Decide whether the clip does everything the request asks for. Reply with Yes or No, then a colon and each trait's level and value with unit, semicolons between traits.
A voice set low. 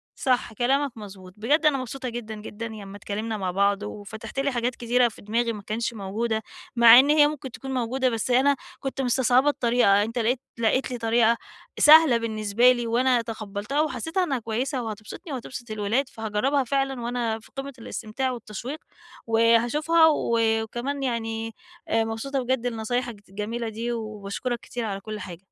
No: high, 235 Hz